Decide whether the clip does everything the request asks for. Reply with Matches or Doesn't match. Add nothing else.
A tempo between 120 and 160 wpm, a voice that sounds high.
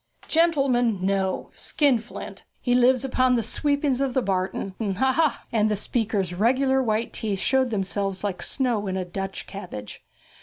Matches